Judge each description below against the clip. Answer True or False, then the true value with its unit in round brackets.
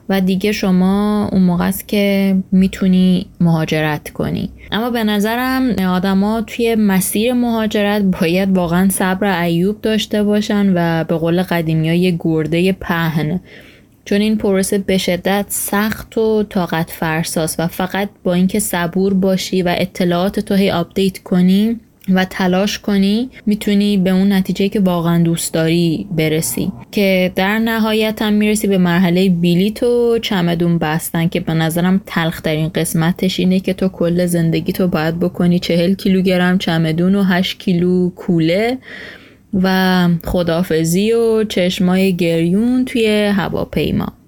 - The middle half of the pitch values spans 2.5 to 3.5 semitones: True (2.9 semitones)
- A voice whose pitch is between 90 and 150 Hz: False (190 Hz)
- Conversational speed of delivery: True (140 wpm)